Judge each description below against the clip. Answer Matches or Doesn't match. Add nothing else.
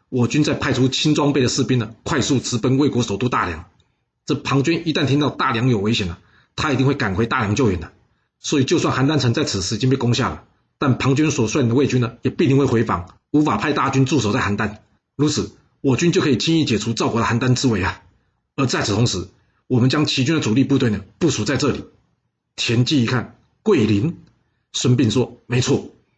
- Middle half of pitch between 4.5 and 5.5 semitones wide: Doesn't match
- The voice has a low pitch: Matches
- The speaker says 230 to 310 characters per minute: Doesn't match